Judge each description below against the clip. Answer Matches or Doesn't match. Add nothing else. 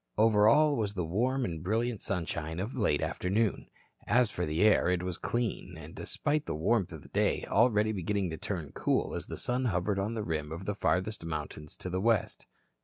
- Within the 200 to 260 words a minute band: Matches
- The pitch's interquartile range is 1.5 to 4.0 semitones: Doesn't match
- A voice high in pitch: Doesn't match